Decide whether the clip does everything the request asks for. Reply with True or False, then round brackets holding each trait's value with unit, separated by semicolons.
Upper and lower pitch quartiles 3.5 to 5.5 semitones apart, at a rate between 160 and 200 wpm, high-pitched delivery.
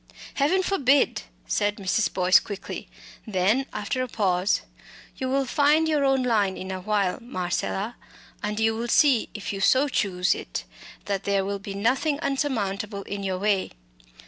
True (5.2 semitones; 165 wpm; 210 Hz)